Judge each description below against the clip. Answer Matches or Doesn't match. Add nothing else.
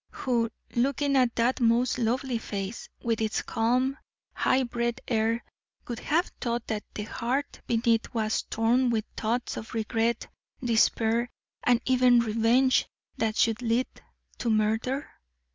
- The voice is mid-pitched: Doesn't match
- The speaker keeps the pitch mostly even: Matches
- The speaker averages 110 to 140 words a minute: Matches